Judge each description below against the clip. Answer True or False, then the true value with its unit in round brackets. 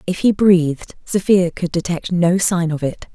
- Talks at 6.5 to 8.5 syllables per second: False (4.5 syllables/s)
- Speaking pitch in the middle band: True (175 Hz)